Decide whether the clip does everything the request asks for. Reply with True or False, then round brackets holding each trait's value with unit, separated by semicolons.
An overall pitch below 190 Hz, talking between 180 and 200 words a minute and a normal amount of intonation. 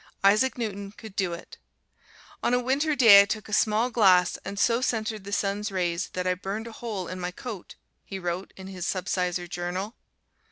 False (200 Hz; 195 wpm; 3.3 semitones)